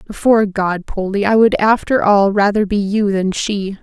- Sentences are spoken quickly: No, average, 190 wpm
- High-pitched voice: Yes, high, 205 Hz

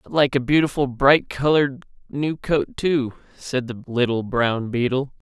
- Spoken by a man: Yes, male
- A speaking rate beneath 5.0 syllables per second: Yes, 4.5 syllables/s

